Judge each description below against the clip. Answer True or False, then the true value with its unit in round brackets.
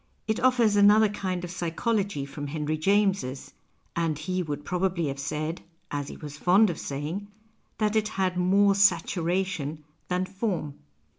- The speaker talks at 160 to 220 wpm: True (165 wpm)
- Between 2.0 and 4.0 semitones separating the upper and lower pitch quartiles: False (4.8 semitones)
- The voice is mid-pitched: True (180 Hz)